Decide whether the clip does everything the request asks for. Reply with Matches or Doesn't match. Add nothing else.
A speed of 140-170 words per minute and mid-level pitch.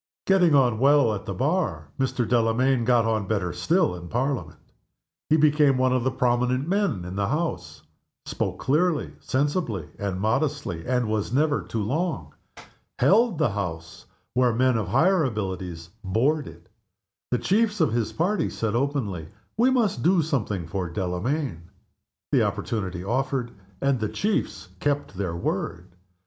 Doesn't match